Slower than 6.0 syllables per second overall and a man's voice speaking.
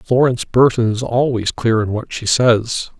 Yes: 4.5 syllables/s; male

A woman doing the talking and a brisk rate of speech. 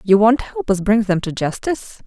Yes: female; fast, 230 wpm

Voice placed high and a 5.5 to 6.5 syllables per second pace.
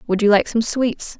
No: high, 220 Hz; 4.9 syllables/s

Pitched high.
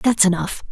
Yes: high, 205 Hz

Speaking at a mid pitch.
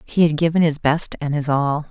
Yes: medium, 155 Hz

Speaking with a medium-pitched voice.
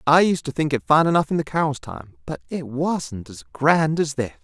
Yes: medium, 145 Hz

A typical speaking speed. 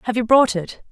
No: fast, 260 wpm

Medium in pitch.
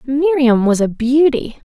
No: very high, 260 Hz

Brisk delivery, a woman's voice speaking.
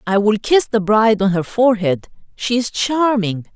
No: average, 185 wpm; female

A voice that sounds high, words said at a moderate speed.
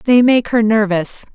Yes: high, 220 Hz; average, 180 wpm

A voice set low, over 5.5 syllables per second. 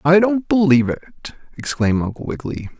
No: medium, 155 Hz; 6.0 syllables/s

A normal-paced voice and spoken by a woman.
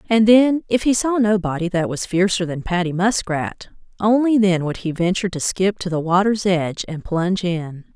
Yes: average, 180 wpm; female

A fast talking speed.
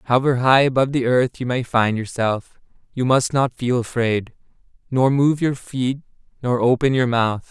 No: average, 175 wpm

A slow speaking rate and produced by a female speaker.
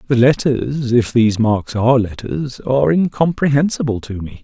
No: slow, 120 wpm; male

